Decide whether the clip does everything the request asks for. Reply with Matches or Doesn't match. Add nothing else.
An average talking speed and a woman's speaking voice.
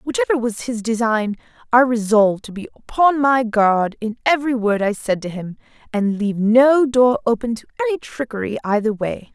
Matches